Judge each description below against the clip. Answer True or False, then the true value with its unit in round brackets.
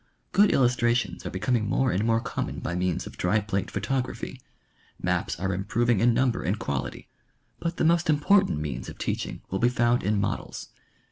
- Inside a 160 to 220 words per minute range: True (185 wpm)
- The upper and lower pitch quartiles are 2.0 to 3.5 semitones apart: False (4.7 semitones)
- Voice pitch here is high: False (115 Hz)